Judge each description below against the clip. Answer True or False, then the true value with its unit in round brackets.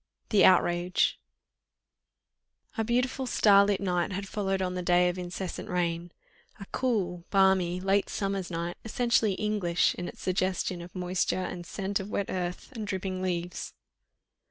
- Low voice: False (185 Hz)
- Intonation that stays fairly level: True (2.1 semitones)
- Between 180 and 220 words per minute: False (145 wpm)